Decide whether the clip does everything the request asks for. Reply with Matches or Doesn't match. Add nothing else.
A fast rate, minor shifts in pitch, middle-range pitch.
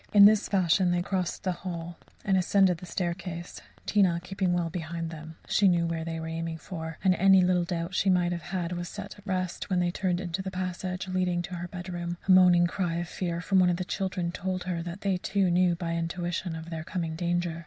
Matches